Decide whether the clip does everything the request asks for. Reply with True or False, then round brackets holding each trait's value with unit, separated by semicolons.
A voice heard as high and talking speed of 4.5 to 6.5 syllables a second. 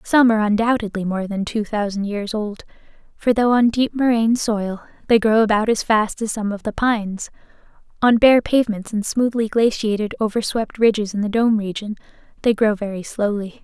True (220 Hz; 5.3 syllables/s)